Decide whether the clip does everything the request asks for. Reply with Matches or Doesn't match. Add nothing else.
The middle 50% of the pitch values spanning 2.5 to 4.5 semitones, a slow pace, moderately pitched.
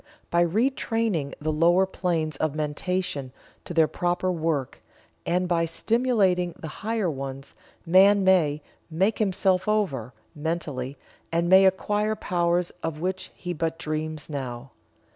Matches